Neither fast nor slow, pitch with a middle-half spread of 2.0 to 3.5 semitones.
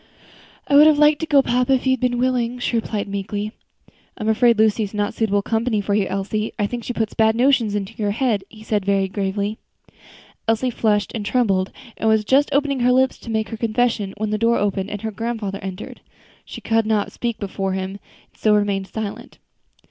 No: fast, 215 wpm; average, 3.0 semitones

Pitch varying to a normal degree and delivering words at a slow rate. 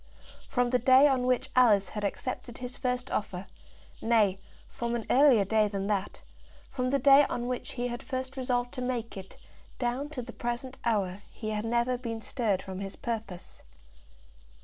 No: average, 3.1 semitones; average, 175 wpm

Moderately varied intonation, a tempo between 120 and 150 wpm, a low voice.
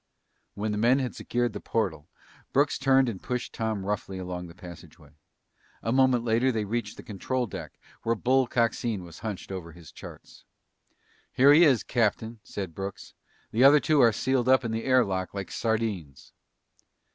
No: average, 4.6 semitones; average, 175 wpm; low, 115 Hz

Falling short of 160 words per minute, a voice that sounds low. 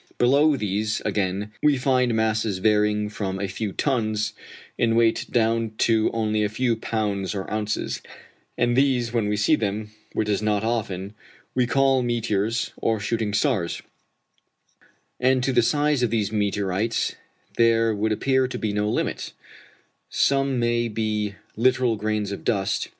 Yes: average, 150 wpm; low, 110 Hz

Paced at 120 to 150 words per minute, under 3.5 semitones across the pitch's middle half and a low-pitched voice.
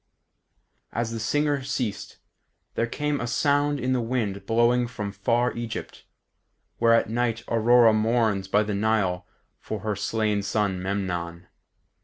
Yes: average, 140 wpm; average, 3.1 semitones; low, 115 Hz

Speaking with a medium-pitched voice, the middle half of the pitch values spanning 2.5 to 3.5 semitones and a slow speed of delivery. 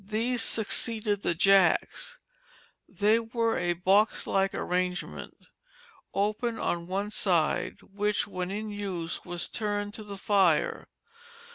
No: high, 200 Hz; average, 2.8 semitones; slow, 120 wpm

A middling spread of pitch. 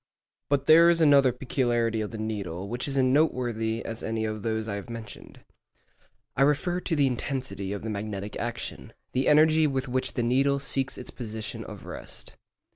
Yes: average, 3.9 semitones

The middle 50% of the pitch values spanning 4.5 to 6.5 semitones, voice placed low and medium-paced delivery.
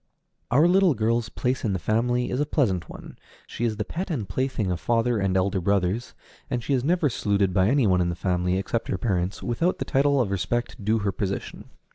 No: average, 4.8 semitones; low, 110 Hz; fast, 225 wpm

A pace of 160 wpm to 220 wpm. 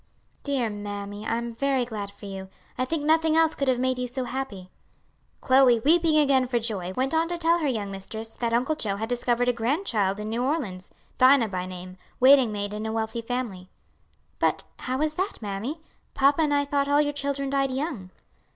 Yes: fast, 205 wpm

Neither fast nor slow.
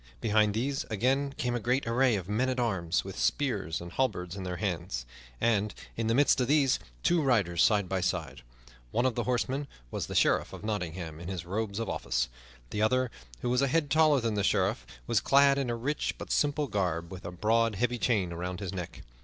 No: fast, 215 wpm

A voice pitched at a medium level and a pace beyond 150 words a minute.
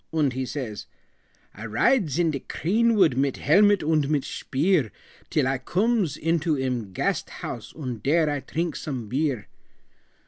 No: medium, 145 Hz; average, 145 wpm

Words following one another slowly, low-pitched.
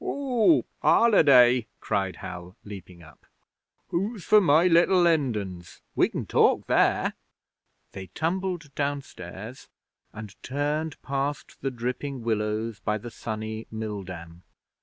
Yes: slow, 115 wpm; low, 120 Hz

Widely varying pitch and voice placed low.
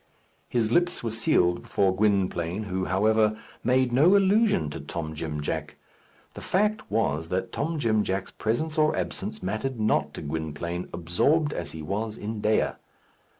Yes: wide, 6.3 semitones; low, 105 Hz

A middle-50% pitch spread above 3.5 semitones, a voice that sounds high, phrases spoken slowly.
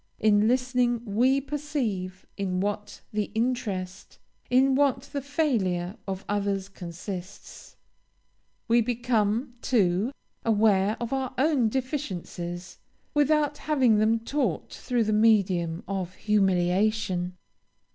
Yes: average, 5.0 semitones; high, 215 Hz; slow, 105 wpm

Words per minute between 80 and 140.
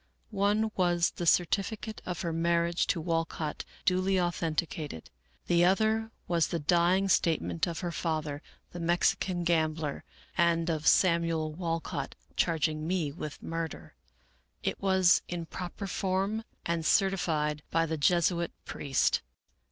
Yes: slow, 135 wpm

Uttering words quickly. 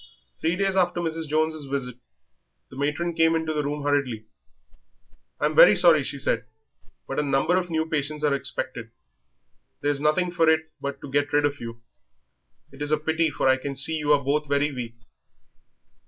No: average, 185 wpm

